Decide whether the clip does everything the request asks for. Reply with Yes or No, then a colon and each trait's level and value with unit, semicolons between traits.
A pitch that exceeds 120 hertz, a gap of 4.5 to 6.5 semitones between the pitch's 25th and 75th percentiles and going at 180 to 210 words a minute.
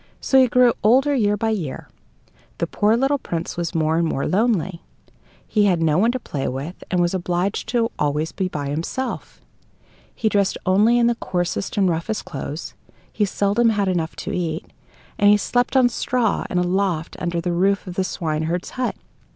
Yes: high, 190 Hz; average, 4.9 semitones; average, 190 wpm